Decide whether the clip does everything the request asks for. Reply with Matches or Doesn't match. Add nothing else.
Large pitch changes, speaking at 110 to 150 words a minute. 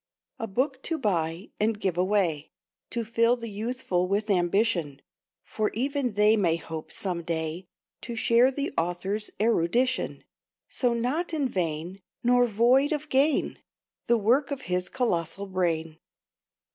Matches